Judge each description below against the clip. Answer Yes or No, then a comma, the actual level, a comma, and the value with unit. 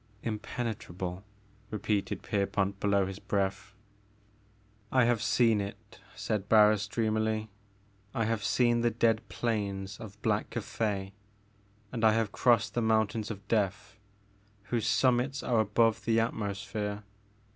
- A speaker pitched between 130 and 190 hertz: No, low, 110 Hz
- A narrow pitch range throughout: Yes, narrow, 2.2 semitones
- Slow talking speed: Yes, slow, 125 wpm